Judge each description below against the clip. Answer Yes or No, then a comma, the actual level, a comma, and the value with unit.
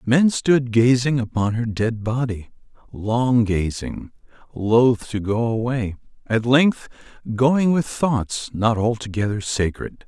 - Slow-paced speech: Yes, slow, 105 wpm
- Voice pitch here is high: No, low, 115 Hz